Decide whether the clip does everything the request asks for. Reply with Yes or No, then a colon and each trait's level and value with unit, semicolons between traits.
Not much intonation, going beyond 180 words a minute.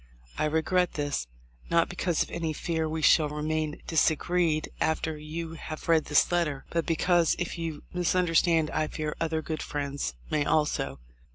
No: narrow, 1.7 semitones; average, 165 wpm